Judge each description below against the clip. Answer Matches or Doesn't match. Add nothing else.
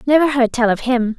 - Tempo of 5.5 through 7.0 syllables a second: Matches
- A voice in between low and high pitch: Doesn't match